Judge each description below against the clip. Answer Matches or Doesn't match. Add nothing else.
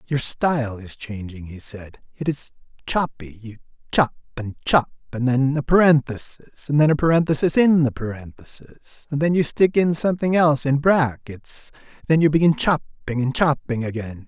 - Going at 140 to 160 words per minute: Matches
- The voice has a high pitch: Doesn't match